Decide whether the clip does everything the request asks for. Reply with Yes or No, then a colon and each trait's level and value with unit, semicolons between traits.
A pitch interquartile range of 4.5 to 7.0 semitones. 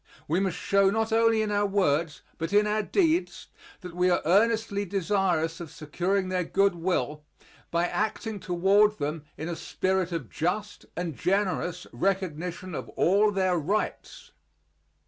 No: average, 3.3 semitones